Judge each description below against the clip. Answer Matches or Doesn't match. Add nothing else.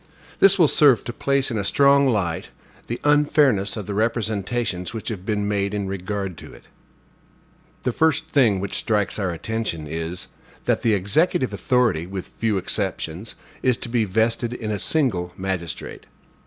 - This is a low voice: Matches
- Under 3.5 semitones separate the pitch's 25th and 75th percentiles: Doesn't match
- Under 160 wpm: Doesn't match